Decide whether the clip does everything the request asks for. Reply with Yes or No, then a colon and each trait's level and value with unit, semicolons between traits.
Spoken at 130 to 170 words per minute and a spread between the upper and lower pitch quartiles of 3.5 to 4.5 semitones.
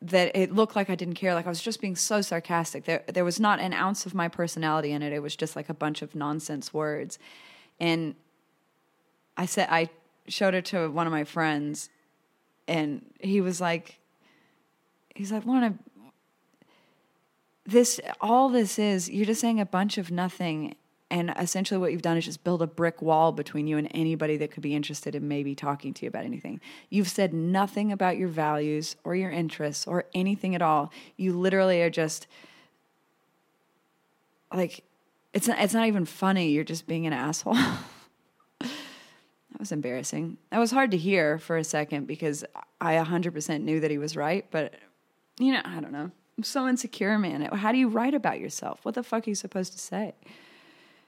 No: average, 185 wpm; average, 3.9 semitones